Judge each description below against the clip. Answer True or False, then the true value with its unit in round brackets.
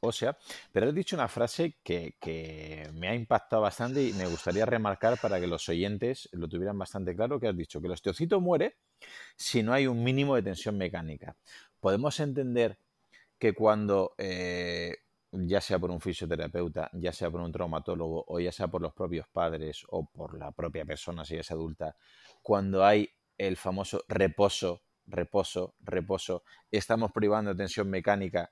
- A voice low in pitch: True (95 Hz)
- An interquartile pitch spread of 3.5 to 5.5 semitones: True (4.2 semitones)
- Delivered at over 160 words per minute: True (175 wpm)